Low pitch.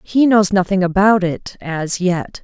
No: high, 190 Hz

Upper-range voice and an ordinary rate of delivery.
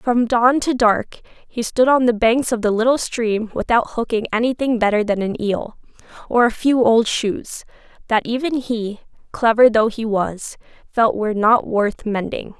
Yes: high, 230 Hz; average, 175 wpm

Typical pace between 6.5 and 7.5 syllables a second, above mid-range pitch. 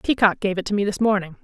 Yes: 6.9 syllables/s; high, 200 Hz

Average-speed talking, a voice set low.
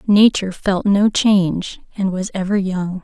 No: average, 160 wpm; high, 190 Hz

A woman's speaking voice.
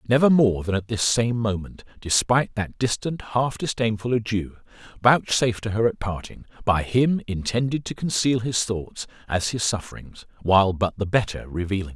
No: male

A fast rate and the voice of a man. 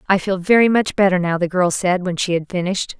No: fast, 260 wpm; female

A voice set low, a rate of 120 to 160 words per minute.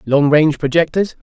No: medium, 155 Hz; slow, 135 wpm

